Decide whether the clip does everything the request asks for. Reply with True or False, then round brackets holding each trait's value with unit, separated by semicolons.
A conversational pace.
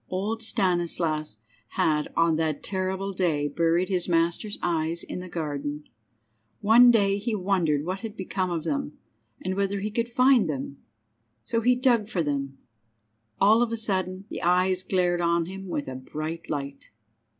True (160 wpm)